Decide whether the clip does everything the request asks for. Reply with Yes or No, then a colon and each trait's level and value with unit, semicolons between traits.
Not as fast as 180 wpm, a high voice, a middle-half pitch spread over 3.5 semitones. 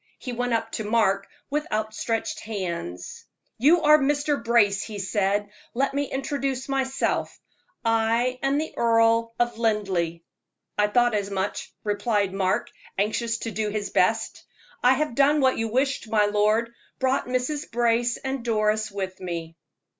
Yes: average, 150 wpm; high, 230 Hz; average, 3.9 semitones